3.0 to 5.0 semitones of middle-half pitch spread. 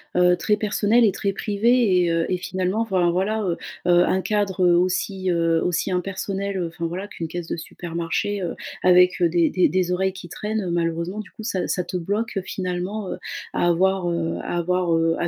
No: narrow, 2.4 semitones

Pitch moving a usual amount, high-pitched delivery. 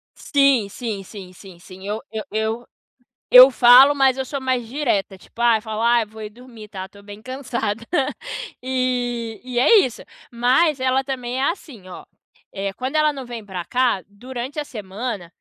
Yes: average, 3.7 semitones; high, 240 Hz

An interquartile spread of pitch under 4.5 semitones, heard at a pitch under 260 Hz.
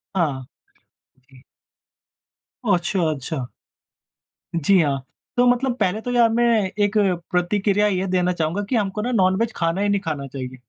No: average, 4.9 semitones; medium, 185 Hz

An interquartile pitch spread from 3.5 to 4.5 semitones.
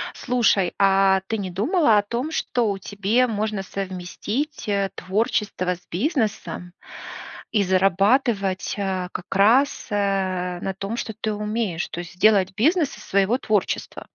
No: average, 3.0 semitones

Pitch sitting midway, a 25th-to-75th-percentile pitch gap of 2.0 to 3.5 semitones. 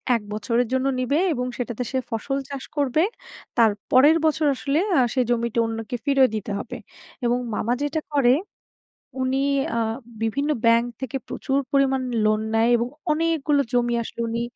No: very high, 250 Hz; average, 3.1 semitones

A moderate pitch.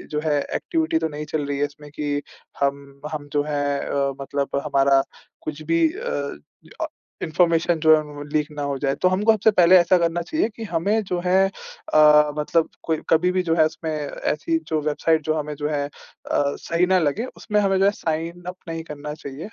Yes: medium, 155 Hz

